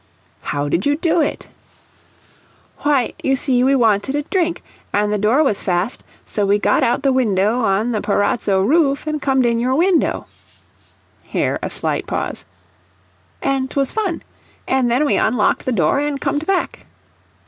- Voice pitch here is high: Yes, very high, 255 Hz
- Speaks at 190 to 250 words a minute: No, average, 165 wpm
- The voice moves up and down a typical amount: No, wide, 5.7 semitones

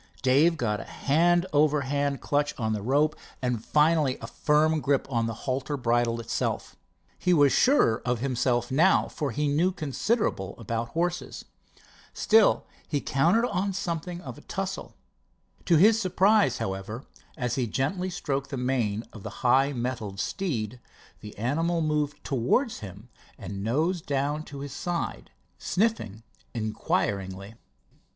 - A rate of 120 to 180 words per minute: Yes, average, 145 wpm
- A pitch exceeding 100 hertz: Yes, medium, 140 Hz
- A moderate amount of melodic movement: No, wide, 6.0 semitones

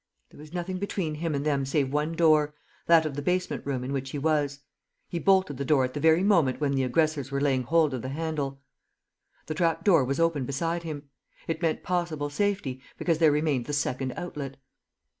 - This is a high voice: No, medium, 150 Hz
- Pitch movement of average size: Yes, average, 3.2 semitones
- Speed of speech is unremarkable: No, fast, 210 wpm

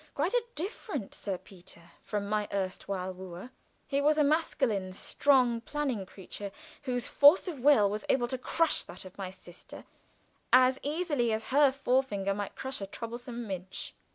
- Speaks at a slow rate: No, average, 160 wpm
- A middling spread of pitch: No, wide, 6.2 semitones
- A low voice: No, high, 235 Hz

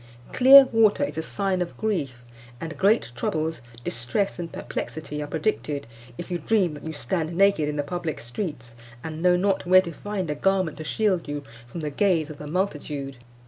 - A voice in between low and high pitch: Yes, medium, 165 Hz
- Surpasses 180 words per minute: Yes, average, 190 wpm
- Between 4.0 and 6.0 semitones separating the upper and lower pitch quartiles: Yes, average, 4.6 semitones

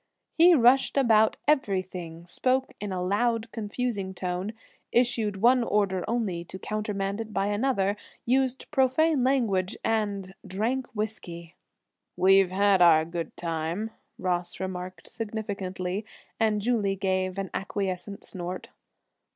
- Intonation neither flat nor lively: Yes, average, 3.8 semitones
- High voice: Yes, high, 200 Hz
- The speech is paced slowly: Yes, slow, 120 wpm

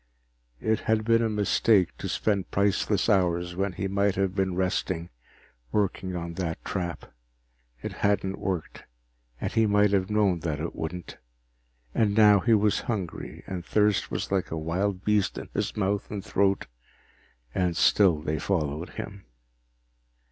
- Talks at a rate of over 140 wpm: Yes, average, 155 wpm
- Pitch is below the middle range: Yes, very low, 95 Hz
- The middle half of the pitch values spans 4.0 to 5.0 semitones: No, average, 2.7 semitones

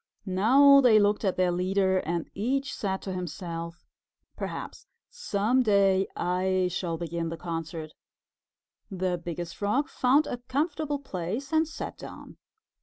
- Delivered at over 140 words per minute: No, slow, 135 wpm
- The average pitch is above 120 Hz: Yes, high, 190 Hz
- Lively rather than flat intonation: Yes, wide, 6.3 semitones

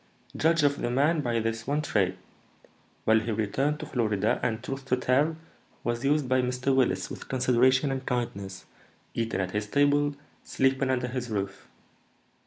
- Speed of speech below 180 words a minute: Yes, average, 165 wpm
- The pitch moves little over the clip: No, average, 3.6 semitones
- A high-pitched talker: No, low, 125 Hz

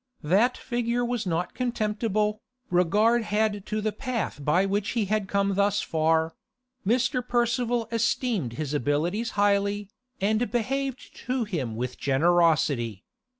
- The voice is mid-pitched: No, high, 205 Hz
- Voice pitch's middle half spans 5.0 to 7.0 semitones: Yes, wide, 5.4 semitones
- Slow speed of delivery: Yes, slow, 130 wpm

